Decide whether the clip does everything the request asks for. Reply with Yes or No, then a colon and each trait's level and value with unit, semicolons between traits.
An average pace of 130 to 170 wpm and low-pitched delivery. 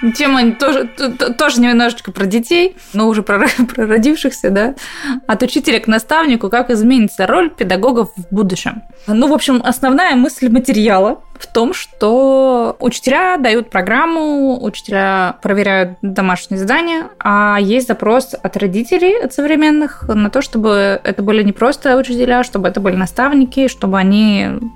No: average, 145 wpm; high, 235 Hz